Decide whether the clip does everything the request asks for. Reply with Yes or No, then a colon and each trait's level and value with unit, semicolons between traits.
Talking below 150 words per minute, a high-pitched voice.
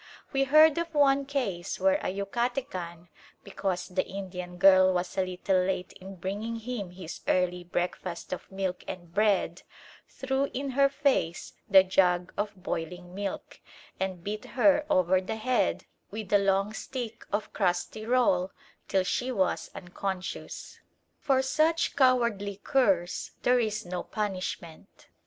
Yes: average, 140 wpm; high, 195 Hz